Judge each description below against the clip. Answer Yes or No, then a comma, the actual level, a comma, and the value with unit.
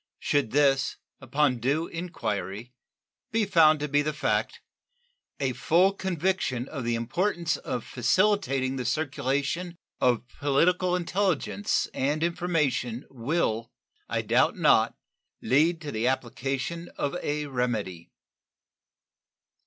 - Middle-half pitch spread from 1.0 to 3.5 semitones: No, average, 5.2 semitones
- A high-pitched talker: No, medium, 145 Hz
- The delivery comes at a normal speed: No, slow, 115 wpm